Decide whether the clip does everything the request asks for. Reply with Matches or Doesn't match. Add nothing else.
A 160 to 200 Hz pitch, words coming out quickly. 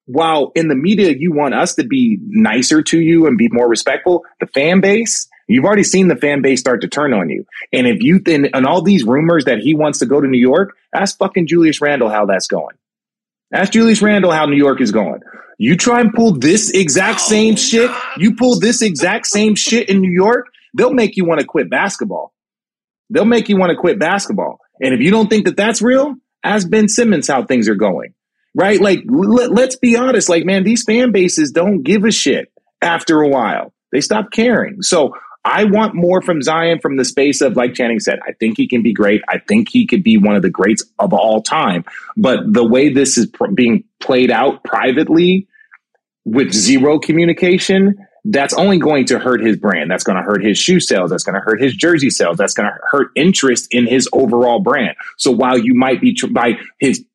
Matches